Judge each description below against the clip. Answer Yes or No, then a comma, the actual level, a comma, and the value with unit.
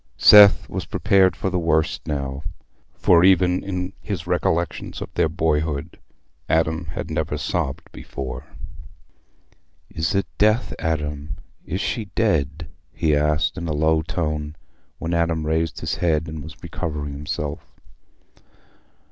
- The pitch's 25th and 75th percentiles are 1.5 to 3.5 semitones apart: Yes, average, 2.8 semitones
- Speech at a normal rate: No, slow, 130 wpm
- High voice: No, very low, 80 Hz